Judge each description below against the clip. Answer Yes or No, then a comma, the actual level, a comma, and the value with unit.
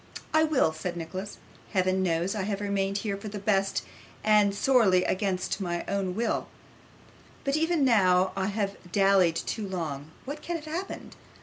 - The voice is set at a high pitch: Yes, high, 195 Hz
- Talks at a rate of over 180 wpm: No, average, 170 wpm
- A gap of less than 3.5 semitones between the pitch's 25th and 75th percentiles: Yes, average, 2.8 semitones